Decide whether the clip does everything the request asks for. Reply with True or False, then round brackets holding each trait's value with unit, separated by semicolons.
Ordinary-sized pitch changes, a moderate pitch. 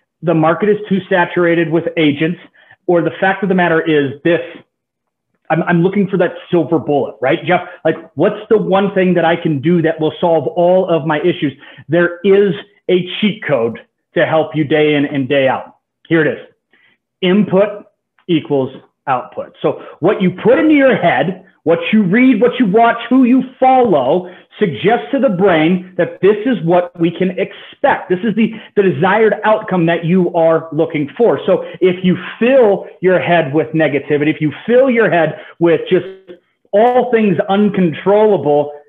True (4.0 semitones; 180 Hz)